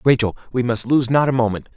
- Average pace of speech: No, fast, 240 wpm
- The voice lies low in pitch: Yes, low, 125 Hz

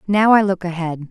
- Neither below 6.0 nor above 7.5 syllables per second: No, 5.2 syllables/s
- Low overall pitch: No, medium, 185 Hz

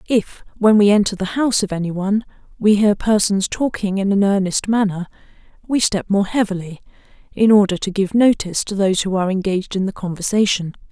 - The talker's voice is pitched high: Yes, high, 200 Hz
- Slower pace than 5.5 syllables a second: No, 6.0 syllables/s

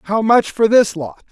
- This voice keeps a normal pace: No, fast, 230 wpm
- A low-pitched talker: No, high, 210 Hz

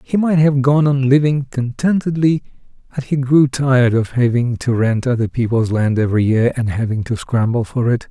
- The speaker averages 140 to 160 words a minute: No, average, 190 wpm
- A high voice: No, low, 130 Hz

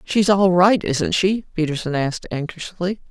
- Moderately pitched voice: Yes, medium, 170 Hz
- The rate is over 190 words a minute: No, average, 155 wpm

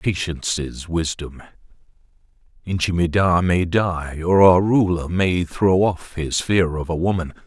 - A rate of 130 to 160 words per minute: Yes, average, 145 wpm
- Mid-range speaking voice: No, very low, 85 Hz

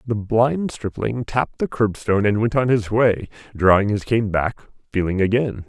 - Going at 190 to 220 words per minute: No, average, 180 wpm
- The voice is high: No, low, 110 Hz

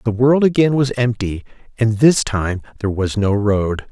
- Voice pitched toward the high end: No, low, 115 Hz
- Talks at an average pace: Yes, average, 185 wpm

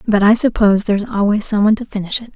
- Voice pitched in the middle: No, high, 210 Hz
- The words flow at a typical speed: No, fast, 255 wpm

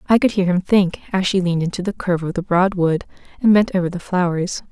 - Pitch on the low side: No, medium, 185 Hz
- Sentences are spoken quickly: Yes, fast, 240 wpm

